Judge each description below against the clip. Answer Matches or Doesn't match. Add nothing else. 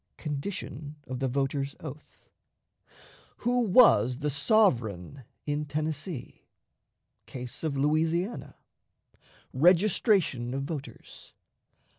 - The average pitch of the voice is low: Doesn't match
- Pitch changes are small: Doesn't match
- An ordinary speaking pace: Doesn't match